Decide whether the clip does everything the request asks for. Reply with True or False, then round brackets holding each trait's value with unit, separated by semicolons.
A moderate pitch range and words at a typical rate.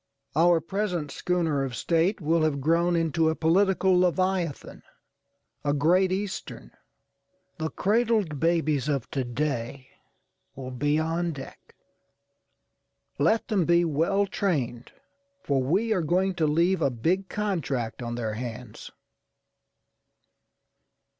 False (4.6 semitones; 115 wpm)